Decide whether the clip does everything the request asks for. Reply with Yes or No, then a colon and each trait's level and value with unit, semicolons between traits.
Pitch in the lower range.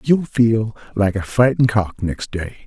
Yes: low, 110 Hz